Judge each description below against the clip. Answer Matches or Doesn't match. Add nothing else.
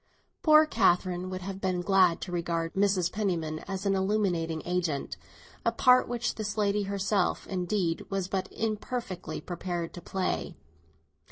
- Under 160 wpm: Matches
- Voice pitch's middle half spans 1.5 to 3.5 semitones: Matches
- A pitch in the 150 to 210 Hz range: Matches